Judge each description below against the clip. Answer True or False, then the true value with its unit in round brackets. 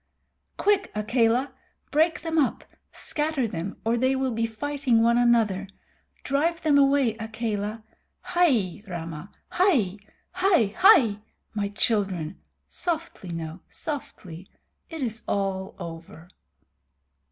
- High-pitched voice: True (230 Hz)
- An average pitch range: False (6.6 semitones)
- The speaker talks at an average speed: False (110 wpm)